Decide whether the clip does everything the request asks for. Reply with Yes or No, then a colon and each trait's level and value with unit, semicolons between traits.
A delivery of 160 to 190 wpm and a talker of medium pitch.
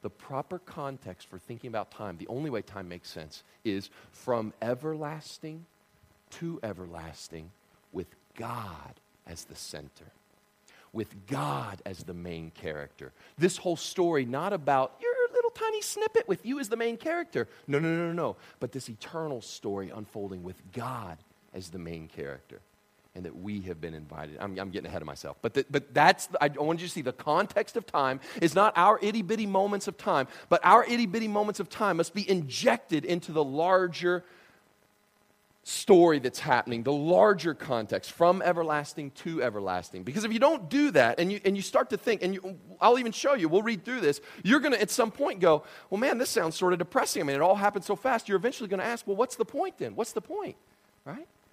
No: average, 200 wpm; medium, 170 Hz